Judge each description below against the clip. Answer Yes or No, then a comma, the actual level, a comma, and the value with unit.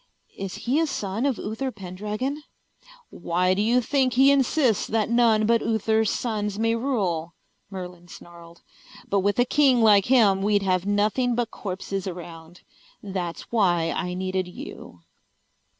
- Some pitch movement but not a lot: Yes, average, 4.5 semitones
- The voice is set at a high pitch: Yes, high, 205 Hz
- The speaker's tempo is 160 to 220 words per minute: No, average, 150 wpm